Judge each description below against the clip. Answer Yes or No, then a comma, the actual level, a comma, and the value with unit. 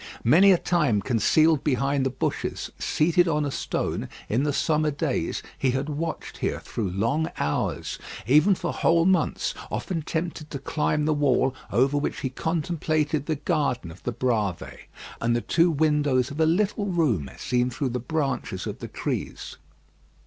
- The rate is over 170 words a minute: No, average, 165 wpm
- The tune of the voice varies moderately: Yes, average, 4.3 semitones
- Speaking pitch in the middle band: Yes, medium, 145 Hz